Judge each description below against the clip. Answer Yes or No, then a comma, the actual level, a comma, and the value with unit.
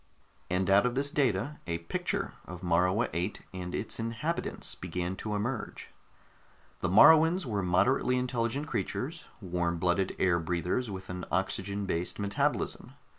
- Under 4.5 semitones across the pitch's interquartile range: No, wide, 5.5 semitones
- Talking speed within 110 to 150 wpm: Yes, average, 140 wpm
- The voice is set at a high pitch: No, low, 100 Hz